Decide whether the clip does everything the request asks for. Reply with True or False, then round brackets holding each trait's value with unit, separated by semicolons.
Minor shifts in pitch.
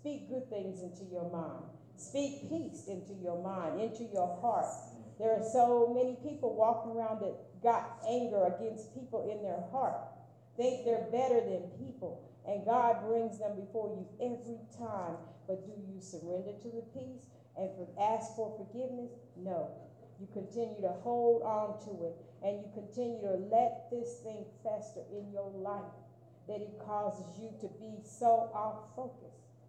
False (3.2 semitones)